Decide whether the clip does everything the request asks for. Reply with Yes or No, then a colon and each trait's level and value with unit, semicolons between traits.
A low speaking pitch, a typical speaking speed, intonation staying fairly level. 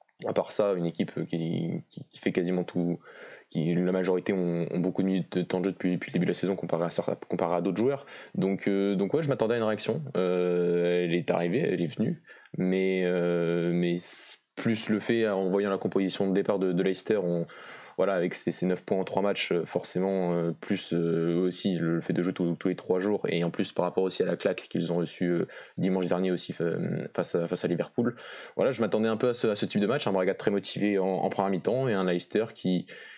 No: very low, 90 Hz; fast, 240 wpm; narrow, 1.9 semitones